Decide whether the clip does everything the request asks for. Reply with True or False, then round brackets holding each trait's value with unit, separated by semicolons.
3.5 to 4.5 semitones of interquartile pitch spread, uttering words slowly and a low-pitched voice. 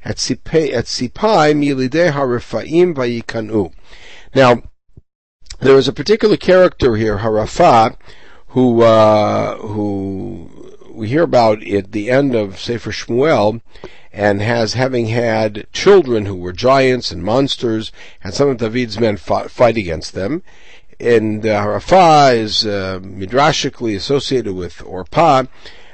True (4.2 semitones; 115 wpm; 115 Hz)